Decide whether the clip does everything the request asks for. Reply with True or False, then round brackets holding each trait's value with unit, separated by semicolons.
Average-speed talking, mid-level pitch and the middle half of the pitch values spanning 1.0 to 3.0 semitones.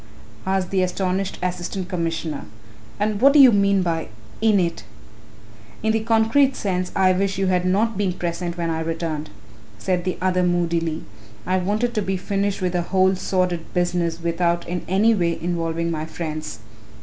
True (170 wpm; 180 Hz; 2.5 semitones)